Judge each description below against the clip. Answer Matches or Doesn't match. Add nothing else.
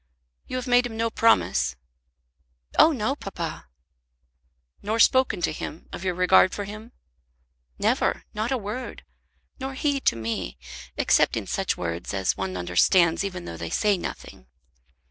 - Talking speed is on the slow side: Doesn't match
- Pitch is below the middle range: Doesn't match